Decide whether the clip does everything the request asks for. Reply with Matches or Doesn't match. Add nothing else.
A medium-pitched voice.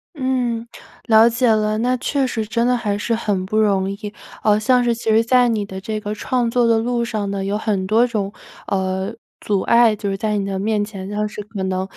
Doesn't match